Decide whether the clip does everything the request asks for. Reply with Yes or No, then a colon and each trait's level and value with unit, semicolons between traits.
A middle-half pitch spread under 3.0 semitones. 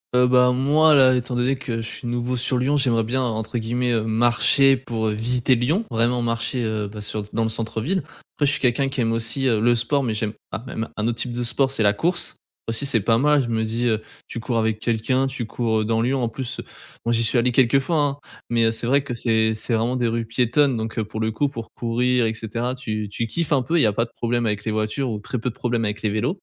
Yes: narrow, 2.4 semitones